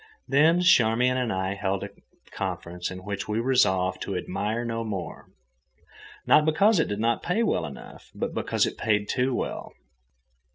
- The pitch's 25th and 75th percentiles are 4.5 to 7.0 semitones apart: Yes, average, 5.3 semitones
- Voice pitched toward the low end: Yes, low, 110 Hz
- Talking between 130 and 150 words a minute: No, average, 160 wpm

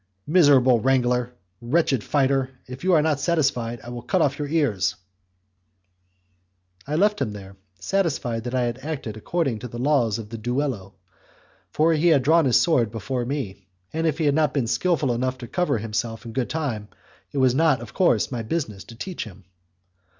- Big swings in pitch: No, average, 4.7 semitones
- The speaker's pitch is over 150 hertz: No, low, 130 Hz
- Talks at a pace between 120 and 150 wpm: No, average, 185 wpm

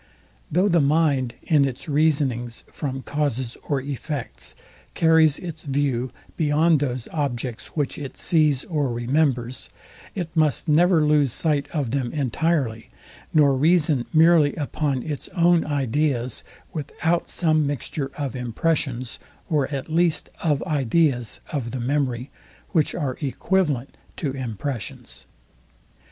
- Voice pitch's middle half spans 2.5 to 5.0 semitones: Yes, average, 3.4 semitones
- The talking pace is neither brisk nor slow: No, slow, 125 wpm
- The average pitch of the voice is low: No, medium, 145 Hz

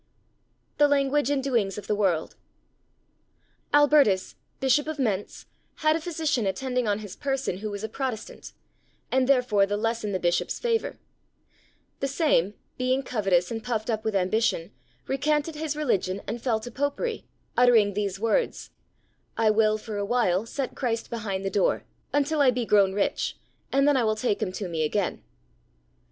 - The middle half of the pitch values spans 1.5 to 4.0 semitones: No, average, 5.3 semitones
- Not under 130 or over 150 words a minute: No, average, 165 wpm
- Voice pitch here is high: Yes, high, 230 Hz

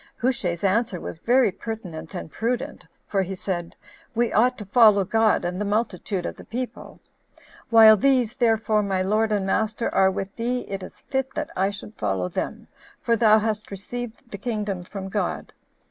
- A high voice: Yes, high, 210 Hz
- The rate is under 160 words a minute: No, average, 175 wpm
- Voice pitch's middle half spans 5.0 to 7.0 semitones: No, average, 3.4 semitones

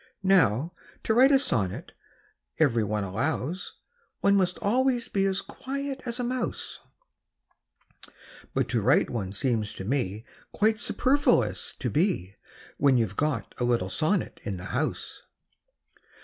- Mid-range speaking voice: Yes, medium, 155 Hz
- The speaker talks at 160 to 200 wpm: No, average, 140 wpm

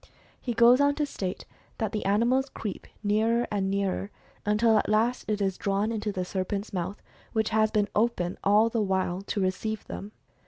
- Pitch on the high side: Yes, high, 210 Hz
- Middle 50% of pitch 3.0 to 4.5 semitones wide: No, narrow, 2.5 semitones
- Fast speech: No, average, 185 wpm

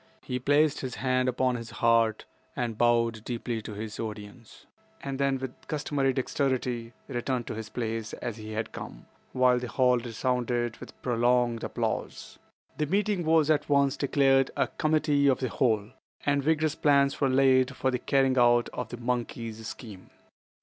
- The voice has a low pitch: Yes, low, 125 Hz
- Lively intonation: No, average, 2.9 semitones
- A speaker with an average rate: Yes, average, 165 wpm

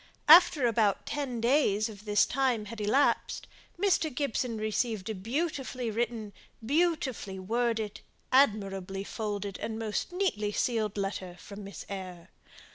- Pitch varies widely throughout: No, average, 4.1 semitones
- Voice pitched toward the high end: Yes, high, 220 Hz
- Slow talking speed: Yes, slow, 125 wpm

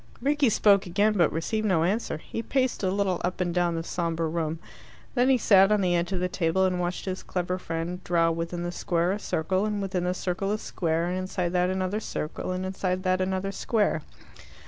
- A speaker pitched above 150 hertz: Yes, medium, 185 Hz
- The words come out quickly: Yes, fast, 215 wpm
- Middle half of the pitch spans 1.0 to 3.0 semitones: Yes, narrow, 2.4 semitones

